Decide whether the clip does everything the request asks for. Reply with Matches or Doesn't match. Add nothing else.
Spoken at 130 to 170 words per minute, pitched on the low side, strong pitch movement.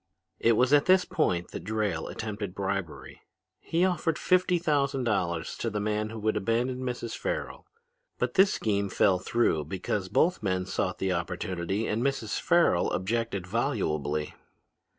Matches